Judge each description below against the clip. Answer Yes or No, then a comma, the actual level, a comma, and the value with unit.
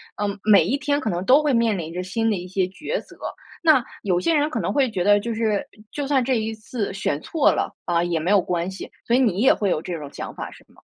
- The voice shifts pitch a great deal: Yes, wide, 6.2 semitones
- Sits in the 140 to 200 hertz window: No, high, 210 Hz